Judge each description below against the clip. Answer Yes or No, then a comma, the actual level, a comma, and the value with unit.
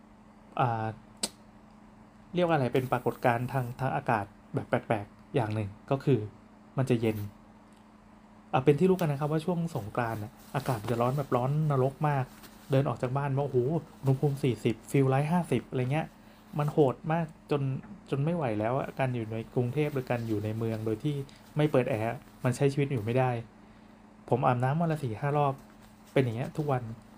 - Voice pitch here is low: Yes, low, 130 Hz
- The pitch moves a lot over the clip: No, average, 4.2 semitones